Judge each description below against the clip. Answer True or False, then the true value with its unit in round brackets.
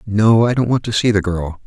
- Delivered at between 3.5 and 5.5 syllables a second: True (5.3 syllables/s)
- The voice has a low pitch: True (105 Hz)